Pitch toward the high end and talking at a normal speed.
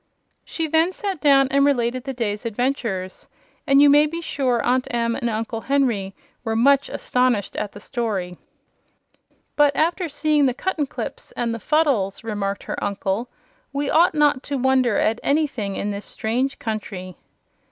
Yes: very high, 250 Hz; average, 160 wpm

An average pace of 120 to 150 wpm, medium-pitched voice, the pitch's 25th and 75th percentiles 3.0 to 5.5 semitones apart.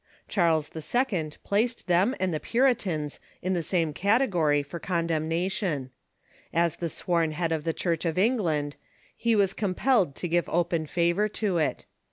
No: average, 160 wpm; medium, 170 Hz; average, 3.9 semitones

